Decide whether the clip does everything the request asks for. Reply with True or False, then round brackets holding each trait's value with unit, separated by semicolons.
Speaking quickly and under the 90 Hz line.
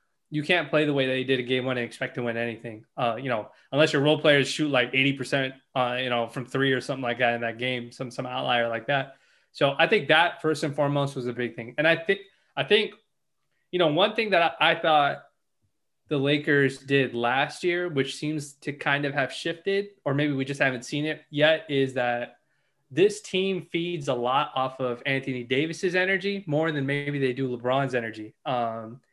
False (220 wpm; 135 Hz)